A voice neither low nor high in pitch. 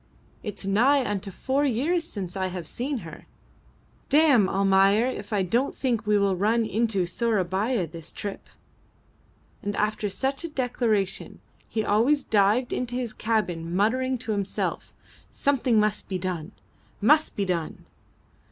No: high, 215 Hz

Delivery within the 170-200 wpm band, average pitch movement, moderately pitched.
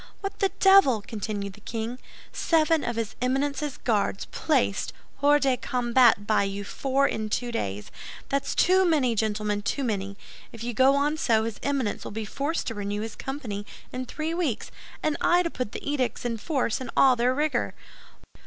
No: average, 180 wpm; average, 4.9 semitones; very high, 250 Hz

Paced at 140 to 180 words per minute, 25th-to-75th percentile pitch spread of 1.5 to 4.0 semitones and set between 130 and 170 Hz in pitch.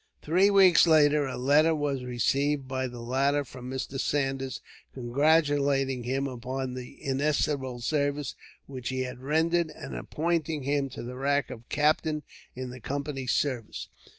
Yes: average, 150 wpm; narrow, 2.5 semitones; medium, 140 Hz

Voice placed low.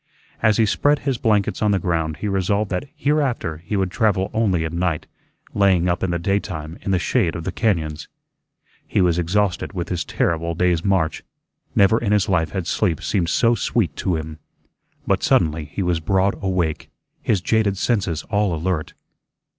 Yes: very low, 95 Hz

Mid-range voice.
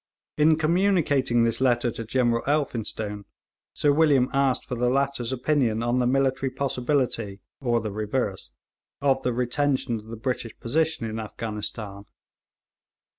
No: low, 125 Hz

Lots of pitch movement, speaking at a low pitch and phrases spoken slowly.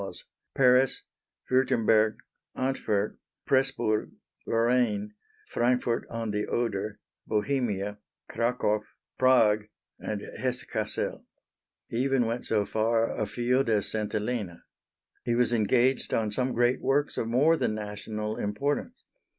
No: average, 3.0 semitones; low, 115 Hz; slow, 110 wpm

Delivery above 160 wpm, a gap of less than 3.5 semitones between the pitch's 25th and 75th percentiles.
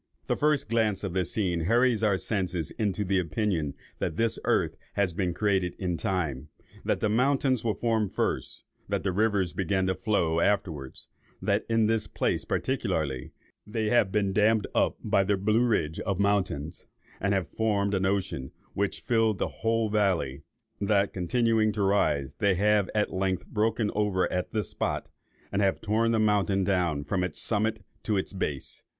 Yes: average, 175 wpm; average, 3.0 semitones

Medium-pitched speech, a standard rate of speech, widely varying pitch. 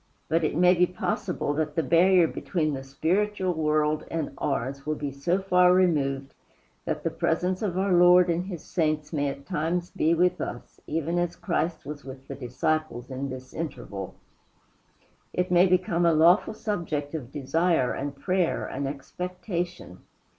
No: medium, 165 Hz; average, 165 wpm; average, 4.0 semitones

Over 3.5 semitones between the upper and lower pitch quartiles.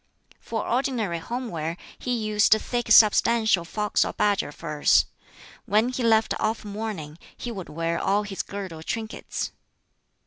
Yes: average, 4.9 semitones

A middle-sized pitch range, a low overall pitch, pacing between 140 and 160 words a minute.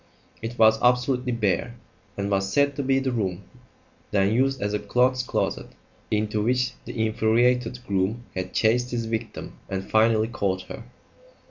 Yes: average, 3.3 semitones; low, 115 Hz; average, 155 wpm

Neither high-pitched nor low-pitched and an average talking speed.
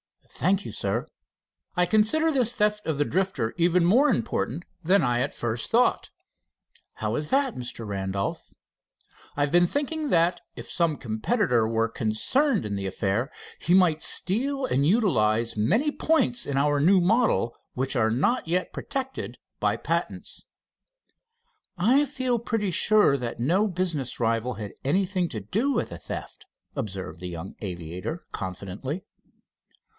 Yes: medium, 165 Hz; average, 150 wpm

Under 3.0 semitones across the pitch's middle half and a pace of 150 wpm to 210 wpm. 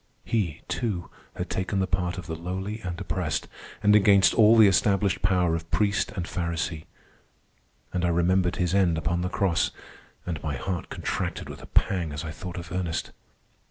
Yes: narrow, 2.6 semitones; average, 180 wpm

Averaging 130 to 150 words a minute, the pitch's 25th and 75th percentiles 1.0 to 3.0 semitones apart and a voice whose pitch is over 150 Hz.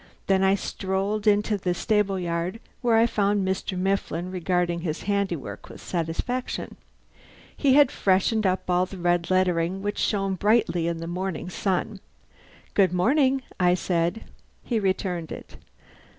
Yes: average, 145 wpm; average, 2.7 semitones; high, 190 Hz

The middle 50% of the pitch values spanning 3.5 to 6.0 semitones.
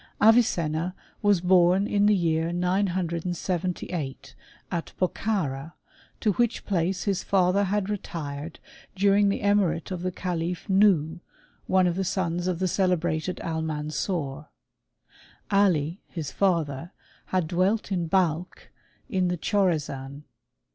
No: average, 3.0 semitones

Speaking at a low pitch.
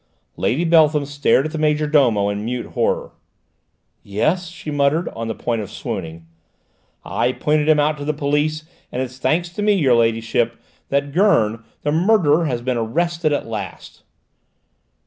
No: medium, 145 Hz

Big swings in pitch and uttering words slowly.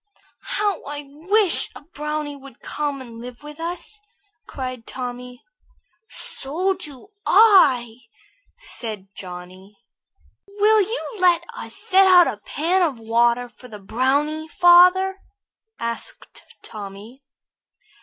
Yes: wide, 7.1 semitones; slow, 115 wpm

